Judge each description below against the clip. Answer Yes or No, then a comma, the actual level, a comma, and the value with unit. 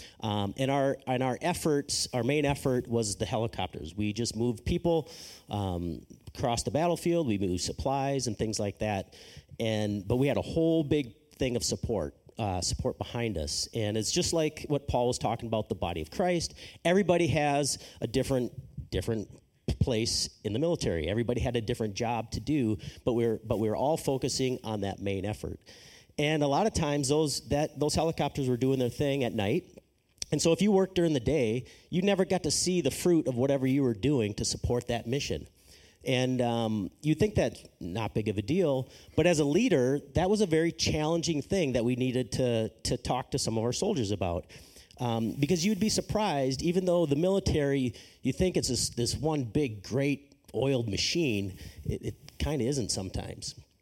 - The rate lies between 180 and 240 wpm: Yes, average, 200 wpm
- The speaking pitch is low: Yes, low, 125 Hz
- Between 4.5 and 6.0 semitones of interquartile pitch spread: Yes, average, 5.3 semitones